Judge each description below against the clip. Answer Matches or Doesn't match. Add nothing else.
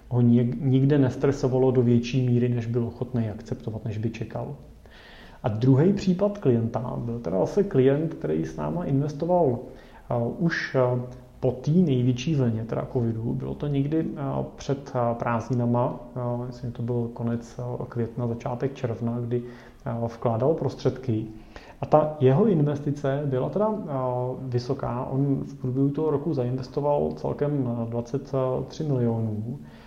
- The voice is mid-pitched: Doesn't match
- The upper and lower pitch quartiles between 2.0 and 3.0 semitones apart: Matches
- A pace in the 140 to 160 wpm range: Doesn't match